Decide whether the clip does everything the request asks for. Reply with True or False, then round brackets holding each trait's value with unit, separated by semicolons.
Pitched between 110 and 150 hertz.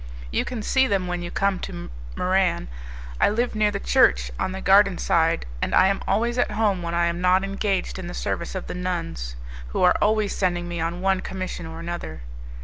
False (185 Hz)